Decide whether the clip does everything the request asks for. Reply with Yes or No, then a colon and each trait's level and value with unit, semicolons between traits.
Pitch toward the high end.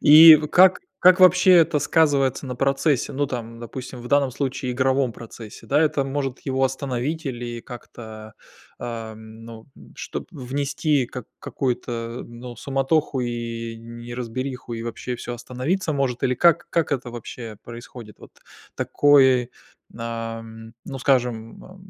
No: low, 125 Hz